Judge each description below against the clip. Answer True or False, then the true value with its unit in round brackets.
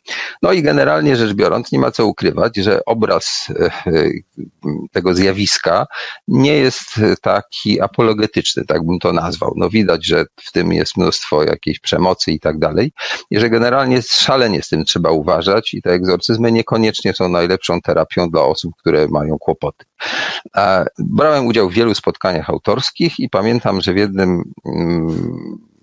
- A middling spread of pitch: True (4.5 semitones)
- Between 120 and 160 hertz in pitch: False (100 Hz)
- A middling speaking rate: True (150 wpm)